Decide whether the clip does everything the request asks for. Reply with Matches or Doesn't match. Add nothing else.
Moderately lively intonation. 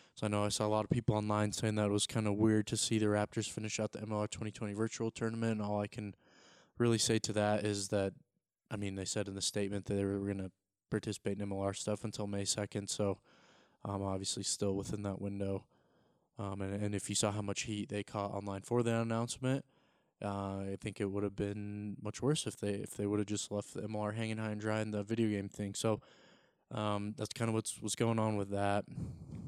Doesn't match